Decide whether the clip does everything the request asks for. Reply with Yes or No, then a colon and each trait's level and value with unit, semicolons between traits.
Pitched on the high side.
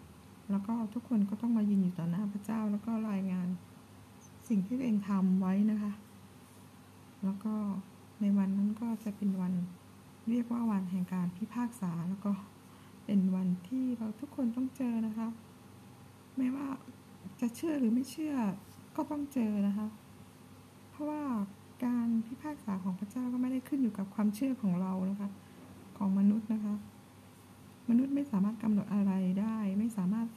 Yes: high, 215 Hz